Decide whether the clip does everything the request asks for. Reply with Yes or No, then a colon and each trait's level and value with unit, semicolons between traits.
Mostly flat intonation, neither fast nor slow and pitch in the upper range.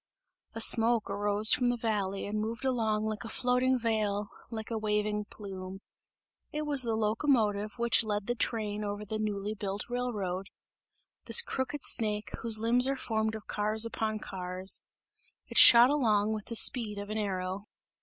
Yes: narrow, 2.2 semitones; average, 165 wpm; high, 215 Hz